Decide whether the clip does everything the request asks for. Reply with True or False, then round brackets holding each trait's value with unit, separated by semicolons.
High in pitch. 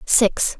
True (220 Hz)